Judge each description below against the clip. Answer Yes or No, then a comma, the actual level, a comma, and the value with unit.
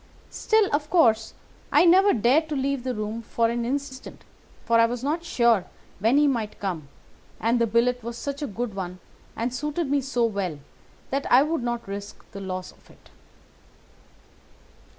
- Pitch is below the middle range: No, high, 240 Hz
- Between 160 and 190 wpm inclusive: Yes, average, 175 wpm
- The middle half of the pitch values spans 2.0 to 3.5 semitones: No, average, 4.3 semitones